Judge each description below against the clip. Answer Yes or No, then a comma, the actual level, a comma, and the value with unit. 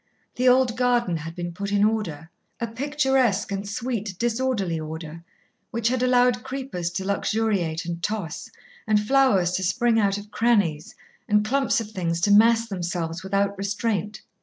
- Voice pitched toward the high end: Yes, high, 210 Hz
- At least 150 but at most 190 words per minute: Yes, average, 160 wpm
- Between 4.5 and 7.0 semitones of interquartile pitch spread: Yes, average, 5.0 semitones